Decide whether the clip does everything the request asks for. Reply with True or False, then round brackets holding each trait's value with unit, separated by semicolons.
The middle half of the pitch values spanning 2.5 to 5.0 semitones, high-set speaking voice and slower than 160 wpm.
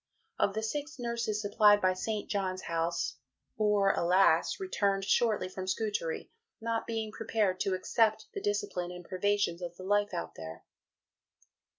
True (2.9 semitones; 205 Hz; 150 wpm)